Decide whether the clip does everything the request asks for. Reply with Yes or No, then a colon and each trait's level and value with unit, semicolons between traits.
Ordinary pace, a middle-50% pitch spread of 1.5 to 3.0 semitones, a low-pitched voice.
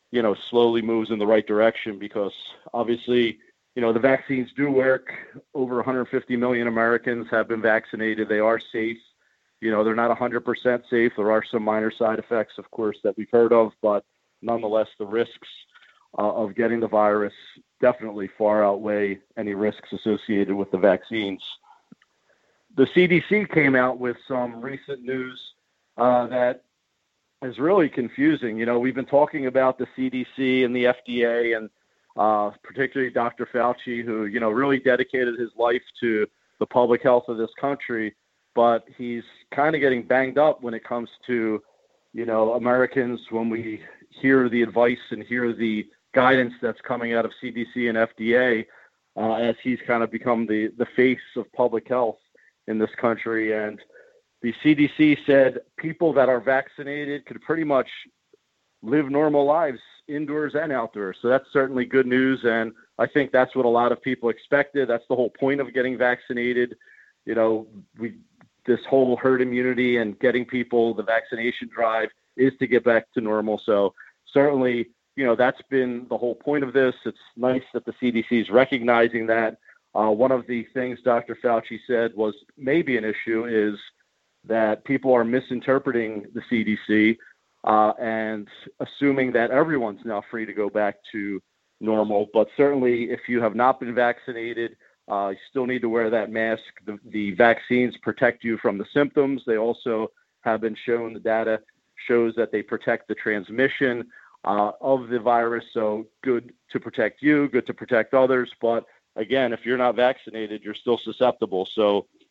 Yes: average, 170 wpm; narrow, 2.4 semitones; low, 120 Hz